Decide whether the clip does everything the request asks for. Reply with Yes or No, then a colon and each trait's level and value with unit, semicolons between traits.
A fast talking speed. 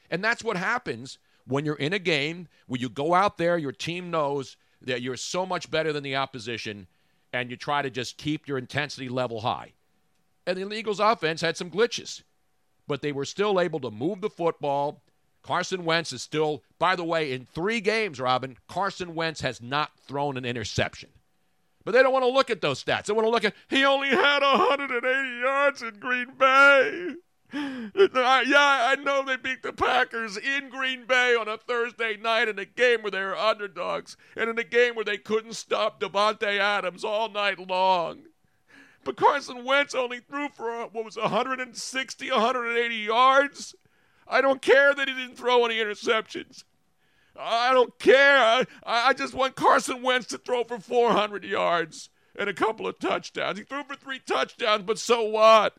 No: average, 185 wpm